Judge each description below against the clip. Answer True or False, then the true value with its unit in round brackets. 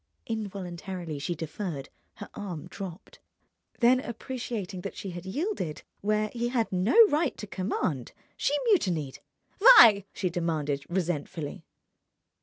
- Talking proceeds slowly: True (120 wpm)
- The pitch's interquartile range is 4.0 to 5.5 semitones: True (5.2 semitones)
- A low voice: False (190 Hz)